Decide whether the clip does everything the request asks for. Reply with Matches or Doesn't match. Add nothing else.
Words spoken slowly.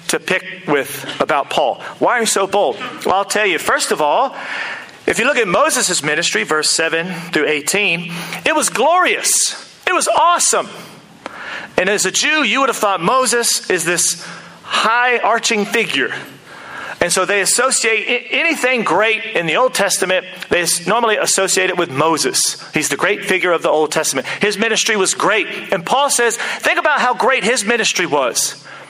Doesn't match